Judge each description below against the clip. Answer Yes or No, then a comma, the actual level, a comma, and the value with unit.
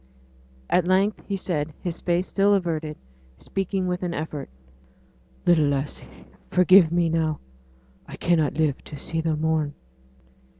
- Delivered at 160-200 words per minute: No, slow, 135 wpm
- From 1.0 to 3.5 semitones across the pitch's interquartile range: Yes, average, 2.8 semitones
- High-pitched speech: No, medium, 165 Hz